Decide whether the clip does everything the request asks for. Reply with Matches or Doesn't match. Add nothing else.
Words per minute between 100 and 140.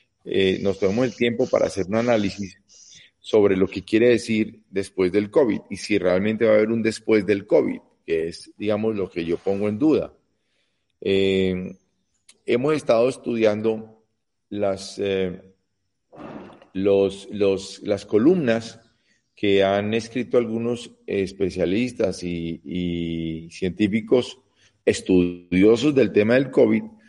Matches